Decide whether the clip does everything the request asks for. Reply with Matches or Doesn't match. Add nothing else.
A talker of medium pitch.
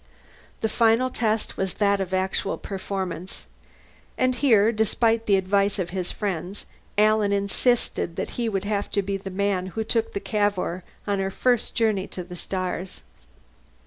Doesn't match